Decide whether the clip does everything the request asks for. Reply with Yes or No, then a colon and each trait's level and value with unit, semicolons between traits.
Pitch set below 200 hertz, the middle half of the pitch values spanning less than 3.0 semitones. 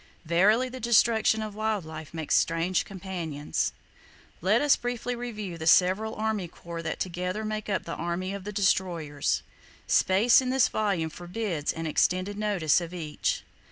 No: high, 190 Hz; average, 4.4 semitones